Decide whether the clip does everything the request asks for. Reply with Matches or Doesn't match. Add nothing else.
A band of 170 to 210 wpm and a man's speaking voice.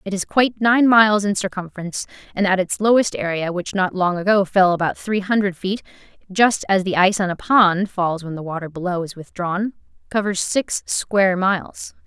Doesn't match